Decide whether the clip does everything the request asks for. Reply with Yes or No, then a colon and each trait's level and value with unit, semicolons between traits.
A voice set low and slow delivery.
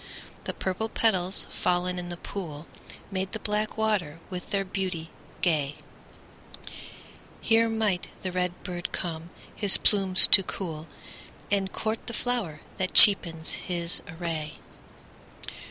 No: medium, 185 Hz; slow, 115 wpm